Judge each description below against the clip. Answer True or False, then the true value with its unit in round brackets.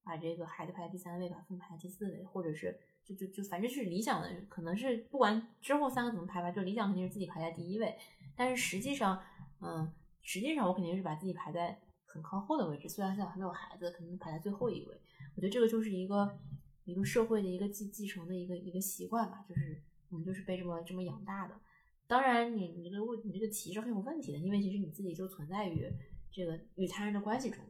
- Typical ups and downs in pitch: True (3.6 semitones)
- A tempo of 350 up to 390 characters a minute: True (380 characters per minute)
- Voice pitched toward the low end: False (190 Hz)